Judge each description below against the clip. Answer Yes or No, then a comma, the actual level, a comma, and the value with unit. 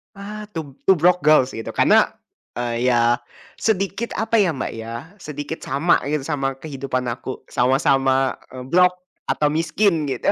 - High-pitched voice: No, medium, 145 Hz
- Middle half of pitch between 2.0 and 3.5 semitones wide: No, wide, 5.4 semitones